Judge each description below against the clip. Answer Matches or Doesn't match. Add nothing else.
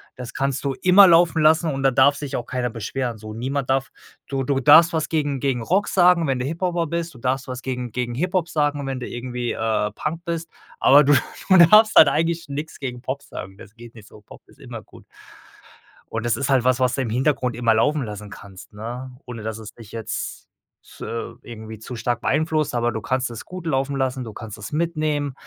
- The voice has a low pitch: Matches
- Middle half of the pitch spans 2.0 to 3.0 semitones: Doesn't match